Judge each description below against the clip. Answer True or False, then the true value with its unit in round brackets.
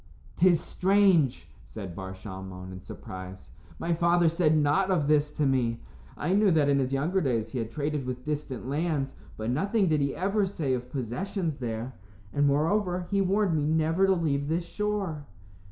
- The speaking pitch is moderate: True (150 Hz)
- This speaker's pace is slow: False (180 wpm)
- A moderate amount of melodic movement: False (5.8 semitones)